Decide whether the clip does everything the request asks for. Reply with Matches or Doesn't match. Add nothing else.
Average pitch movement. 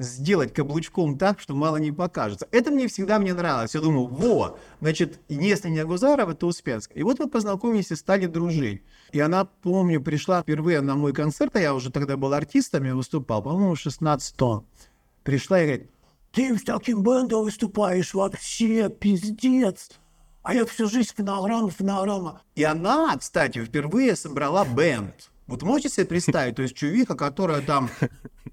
Doesn't match